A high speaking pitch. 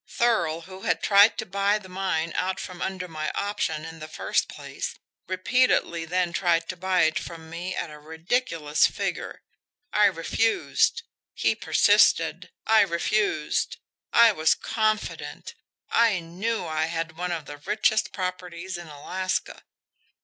No: medium, 180 Hz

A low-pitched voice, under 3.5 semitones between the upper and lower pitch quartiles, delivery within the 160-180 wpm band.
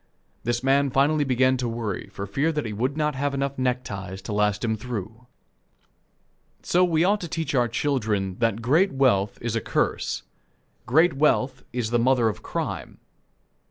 No: low, 125 Hz; average, 4.1 semitones; average, 165 wpm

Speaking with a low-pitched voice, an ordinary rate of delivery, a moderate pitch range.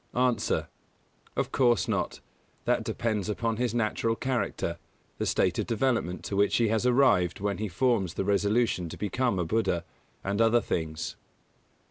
Yes: low, 110 Hz; average, 160 wpm; average, 3.7 semitones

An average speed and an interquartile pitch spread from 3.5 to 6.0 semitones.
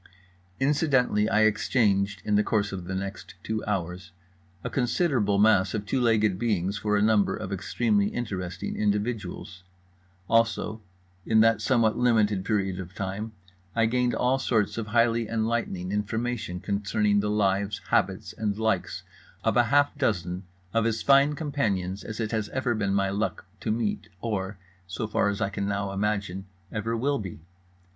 No: average, 160 wpm; average, 2.7 semitones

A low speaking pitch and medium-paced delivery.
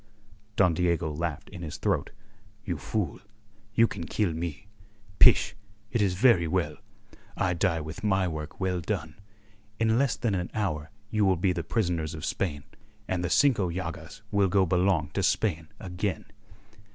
Yes: very low, 90 Hz; average, 165 wpm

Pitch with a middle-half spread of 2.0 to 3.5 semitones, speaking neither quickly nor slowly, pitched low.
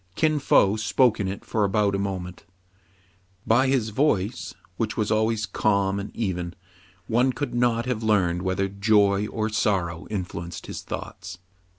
Yes: average, 2.8 semitones; average, 155 wpm; low, 105 Hz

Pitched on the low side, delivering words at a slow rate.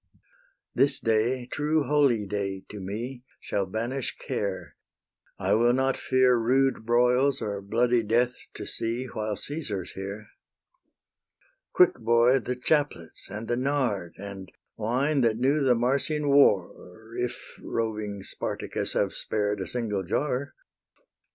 Yes: low, 120 Hz; slow, 125 wpm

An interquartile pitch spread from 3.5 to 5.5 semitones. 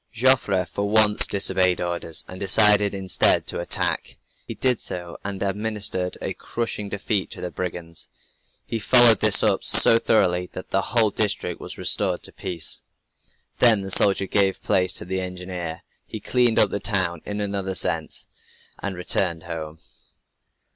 No: narrow, 2.6 semitones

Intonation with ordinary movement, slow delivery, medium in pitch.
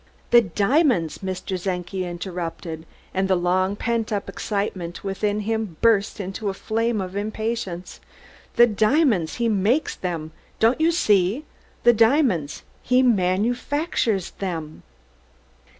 No: average, 4.1 semitones; slow, 120 wpm; high, 200 Hz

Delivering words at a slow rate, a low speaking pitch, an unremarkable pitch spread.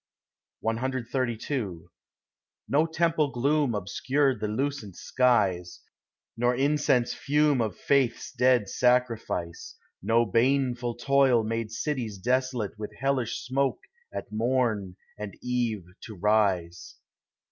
Yes: slow, 105 wpm; low, 120 Hz; average, 3.8 semitones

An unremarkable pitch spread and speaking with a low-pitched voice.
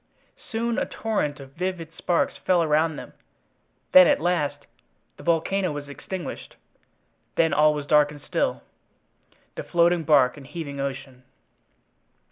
No: average, 3.3 semitones; medium, 155 Hz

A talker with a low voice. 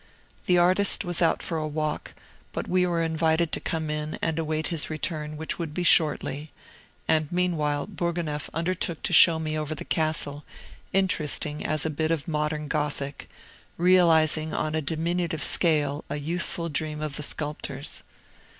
No: medium, 155 Hz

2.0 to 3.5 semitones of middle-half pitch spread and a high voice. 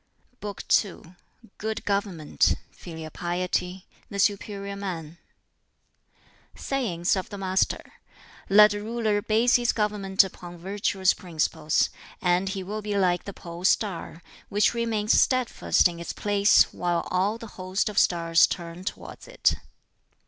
Yes: average, 3.0 semitones; high, 195 Hz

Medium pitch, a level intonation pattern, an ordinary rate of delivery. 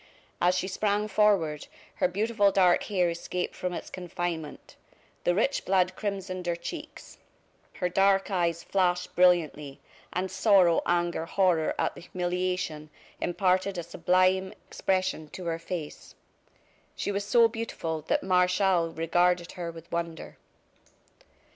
No: medium, 180 Hz; narrow, 2.1 semitones; slow, 130 wpm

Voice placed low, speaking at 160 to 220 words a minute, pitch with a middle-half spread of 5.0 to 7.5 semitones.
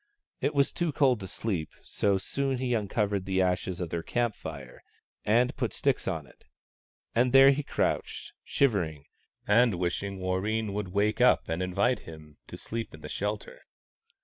Yes: low, 105 Hz; average, 170 wpm; average, 5.3 semitones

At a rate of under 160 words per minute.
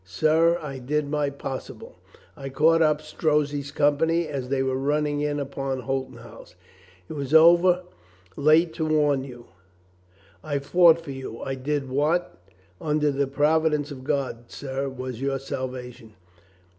Yes: average, 150 wpm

